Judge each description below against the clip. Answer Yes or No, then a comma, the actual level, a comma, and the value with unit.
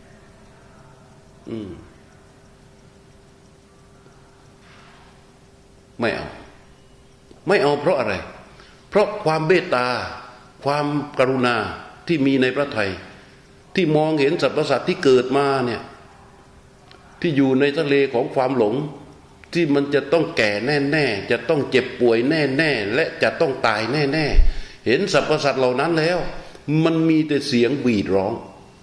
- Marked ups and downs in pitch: No, average, 3.9 semitones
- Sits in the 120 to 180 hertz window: Yes, medium, 140 Hz